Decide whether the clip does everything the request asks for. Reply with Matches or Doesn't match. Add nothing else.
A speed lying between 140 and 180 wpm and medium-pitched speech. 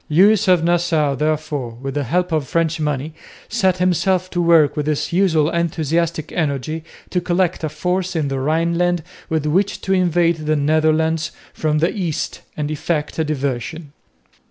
Matches